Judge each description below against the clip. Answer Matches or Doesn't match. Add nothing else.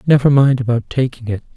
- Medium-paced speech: Matches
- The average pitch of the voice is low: Matches